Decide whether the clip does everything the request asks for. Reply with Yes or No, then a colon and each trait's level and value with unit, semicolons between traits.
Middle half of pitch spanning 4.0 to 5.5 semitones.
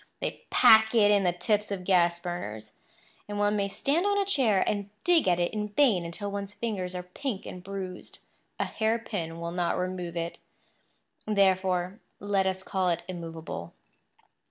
No: average, 2.9 semitones